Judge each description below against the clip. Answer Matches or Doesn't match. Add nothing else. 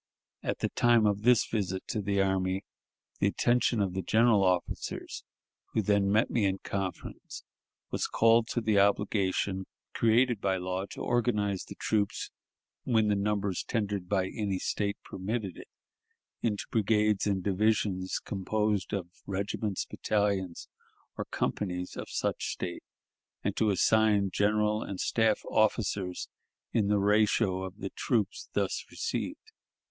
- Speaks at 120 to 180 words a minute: Matches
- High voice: Doesn't match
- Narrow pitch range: Matches